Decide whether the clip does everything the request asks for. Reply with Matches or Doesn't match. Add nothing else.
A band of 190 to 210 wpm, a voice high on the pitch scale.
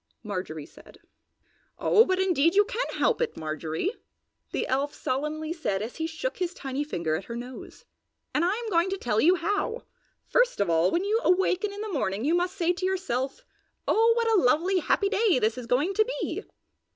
Matches